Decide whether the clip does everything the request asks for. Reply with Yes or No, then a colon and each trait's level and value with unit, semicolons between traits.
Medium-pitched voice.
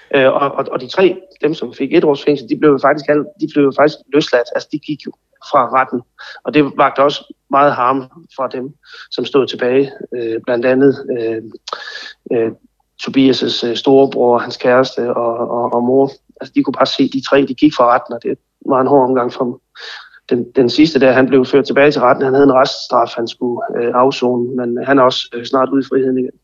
No: low, 130 Hz